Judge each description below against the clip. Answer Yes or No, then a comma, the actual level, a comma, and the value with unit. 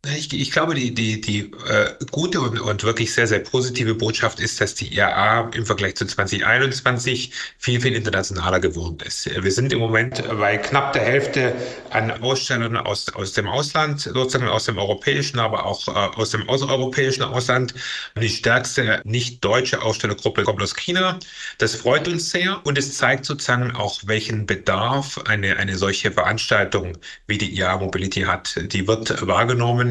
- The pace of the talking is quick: No, average, 165 wpm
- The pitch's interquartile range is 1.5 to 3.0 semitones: No, average, 4.1 semitones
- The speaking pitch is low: Yes, low, 115 Hz